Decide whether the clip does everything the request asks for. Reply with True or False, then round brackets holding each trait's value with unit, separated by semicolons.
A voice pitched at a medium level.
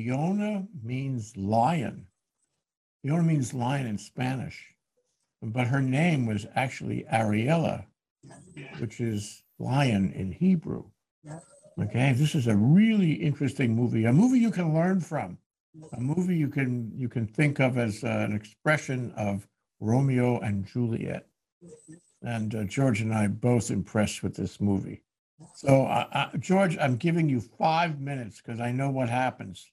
False (130 Hz)